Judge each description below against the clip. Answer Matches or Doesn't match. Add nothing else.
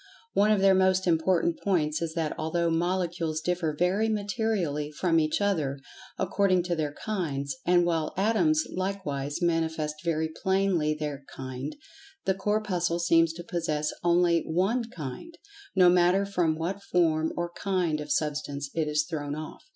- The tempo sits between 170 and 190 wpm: Doesn't match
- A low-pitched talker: Doesn't match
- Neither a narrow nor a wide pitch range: Matches